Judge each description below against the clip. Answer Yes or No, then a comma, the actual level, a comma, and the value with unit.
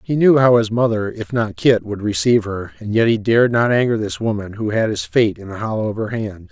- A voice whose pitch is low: Yes, low, 110 Hz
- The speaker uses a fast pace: Yes, fast, 265 wpm